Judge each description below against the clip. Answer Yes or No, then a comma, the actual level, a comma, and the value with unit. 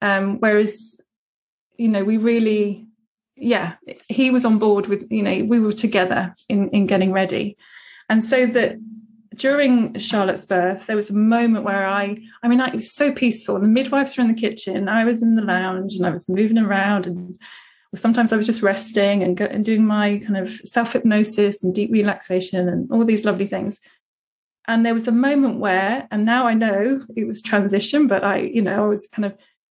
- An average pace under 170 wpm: No, fast, 205 wpm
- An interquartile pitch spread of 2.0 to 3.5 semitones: Yes, narrow, 2.5 semitones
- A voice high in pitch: Yes, high, 215 Hz